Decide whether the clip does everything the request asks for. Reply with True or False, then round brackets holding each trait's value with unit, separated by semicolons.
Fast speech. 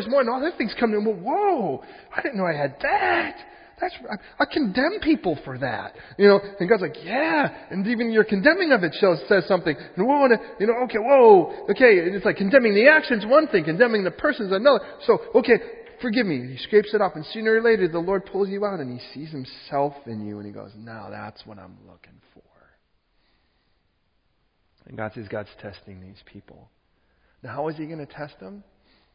True (210 wpm)